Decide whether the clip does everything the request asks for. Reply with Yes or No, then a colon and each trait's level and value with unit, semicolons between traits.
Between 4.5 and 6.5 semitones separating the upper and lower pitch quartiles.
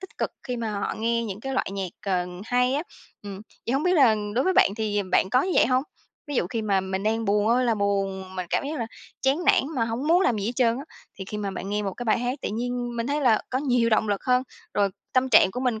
No: average, 3.9 semitones